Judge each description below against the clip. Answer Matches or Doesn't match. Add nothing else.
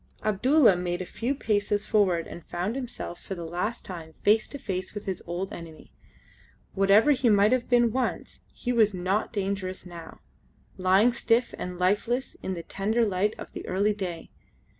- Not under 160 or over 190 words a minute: Matches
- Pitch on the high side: Matches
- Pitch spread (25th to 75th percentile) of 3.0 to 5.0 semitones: Matches